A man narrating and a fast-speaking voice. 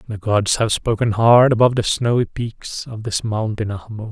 No: male; average, 190 wpm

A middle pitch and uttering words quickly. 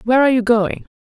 No: high, 230 Hz; fast, 235 wpm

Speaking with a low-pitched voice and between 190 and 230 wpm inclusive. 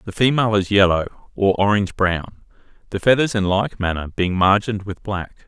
No: low, 100 Hz; average, 175 wpm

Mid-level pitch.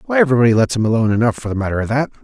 No: low, 120 Hz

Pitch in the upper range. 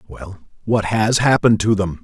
No: low, 105 Hz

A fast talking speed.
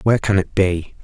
Yes: fast, 230 wpm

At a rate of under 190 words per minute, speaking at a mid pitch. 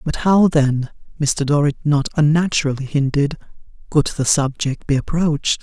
Yes: average, 140 wpm; medium, 145 Hz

